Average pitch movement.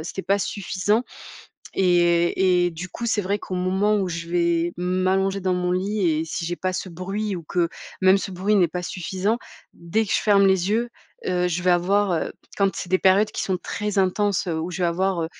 No: narrow, 2.1 semitones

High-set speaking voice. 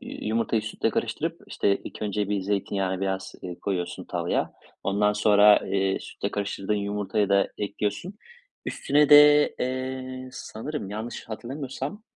No: low, 105 Hz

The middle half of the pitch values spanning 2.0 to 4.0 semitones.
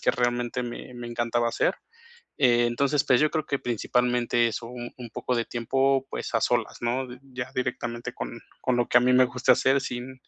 No: narrow, 1.3 semitones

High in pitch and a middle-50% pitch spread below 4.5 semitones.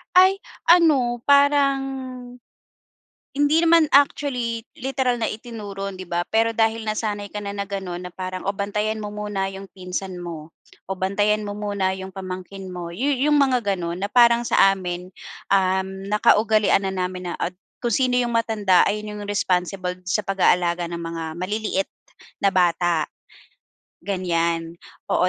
Yes: high, 200 Hz; average, 3.8 semitones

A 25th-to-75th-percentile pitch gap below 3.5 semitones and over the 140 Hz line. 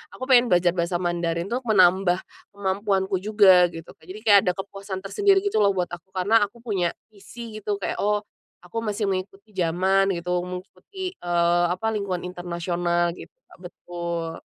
Yes: average, 2.9 semitones; high, 190 Hz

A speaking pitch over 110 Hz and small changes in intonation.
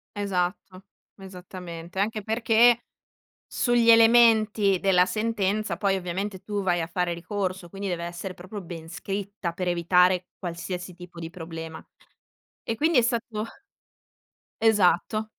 No: high, 190 Hz; average, 3.4 semitones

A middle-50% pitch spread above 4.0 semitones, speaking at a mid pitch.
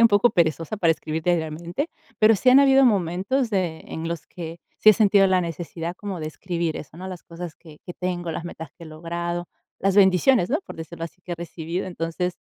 No: average, 2.9 semitones; medium, 175 Hz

